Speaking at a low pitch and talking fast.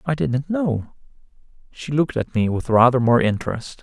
No: low, 130 Hz; average, 170 wpm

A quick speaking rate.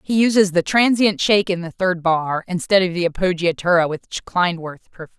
No: average, 185 wpm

